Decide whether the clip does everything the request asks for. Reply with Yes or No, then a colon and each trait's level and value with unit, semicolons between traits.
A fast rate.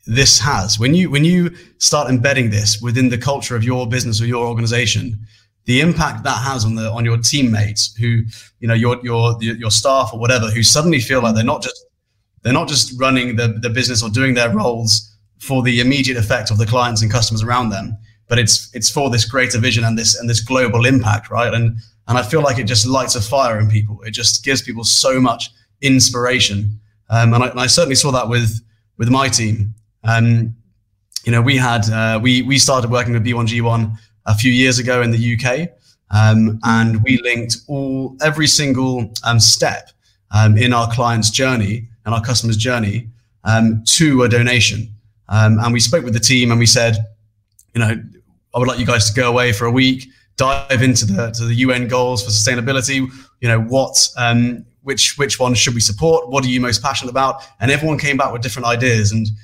Yes: fast, 210 wpm